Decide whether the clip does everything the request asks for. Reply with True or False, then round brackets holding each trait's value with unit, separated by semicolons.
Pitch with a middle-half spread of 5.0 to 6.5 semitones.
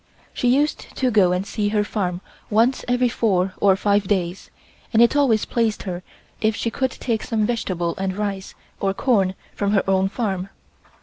False (3.4 semitones)